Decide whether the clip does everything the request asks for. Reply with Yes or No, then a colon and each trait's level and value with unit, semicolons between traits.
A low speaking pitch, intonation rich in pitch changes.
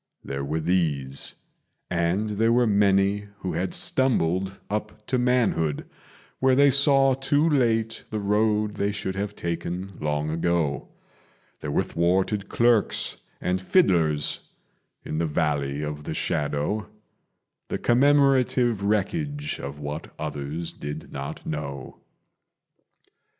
Yes: very low, 95 Hz; wide, 6.7 semitones